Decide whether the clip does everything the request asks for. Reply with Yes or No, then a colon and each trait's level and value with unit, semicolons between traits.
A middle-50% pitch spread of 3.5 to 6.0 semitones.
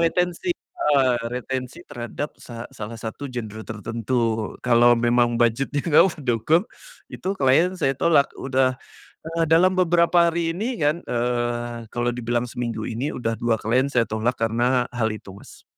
Yes: average, 4.4 semitones